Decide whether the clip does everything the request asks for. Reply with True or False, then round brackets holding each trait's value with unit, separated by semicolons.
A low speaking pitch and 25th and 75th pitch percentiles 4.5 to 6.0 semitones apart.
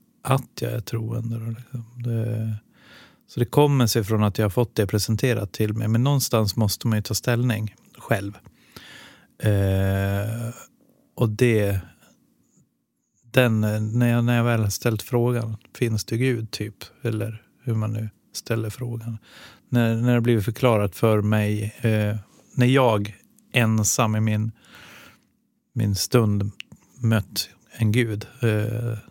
False (115 Hz; 2.0 semitones)